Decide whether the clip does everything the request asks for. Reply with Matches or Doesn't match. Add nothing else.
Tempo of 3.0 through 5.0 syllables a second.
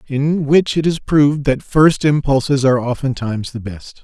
Matches